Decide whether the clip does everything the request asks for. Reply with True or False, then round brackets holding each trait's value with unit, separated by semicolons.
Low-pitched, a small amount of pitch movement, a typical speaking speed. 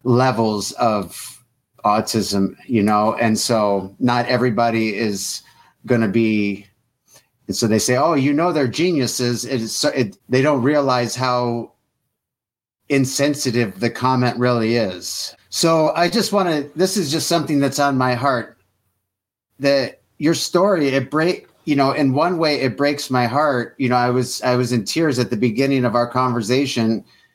False (125 Hz; 3.7 semitones; 165 wpm)